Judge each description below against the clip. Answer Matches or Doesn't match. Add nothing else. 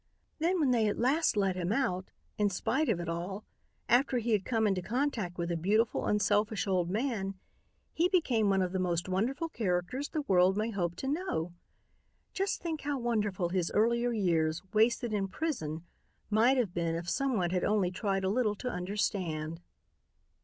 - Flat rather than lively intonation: Doesn't match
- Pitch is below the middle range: Doesn't match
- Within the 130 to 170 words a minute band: Doesn't match